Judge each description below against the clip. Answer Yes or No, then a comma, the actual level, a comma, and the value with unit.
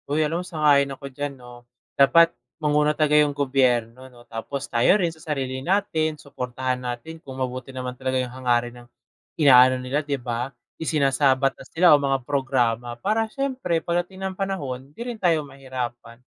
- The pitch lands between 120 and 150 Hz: Yes, low, 135 Hz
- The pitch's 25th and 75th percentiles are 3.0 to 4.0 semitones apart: Yes, average, 3.6 semitones